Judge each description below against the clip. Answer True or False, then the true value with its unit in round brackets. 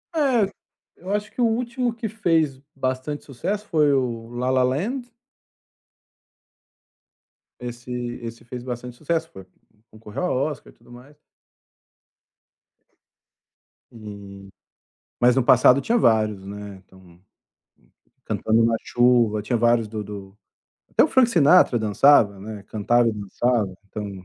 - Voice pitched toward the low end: True (120 Hz)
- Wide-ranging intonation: True (5.9 semitones)